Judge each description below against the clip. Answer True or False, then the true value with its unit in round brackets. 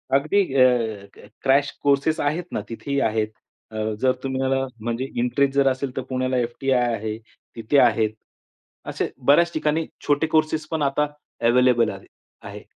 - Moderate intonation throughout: True (3.5 semitones)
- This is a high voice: False (130 Hz)